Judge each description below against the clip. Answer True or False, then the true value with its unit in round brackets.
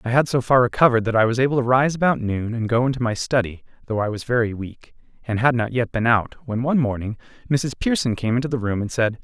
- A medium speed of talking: False (260 wpm)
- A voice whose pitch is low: True (120 Hz)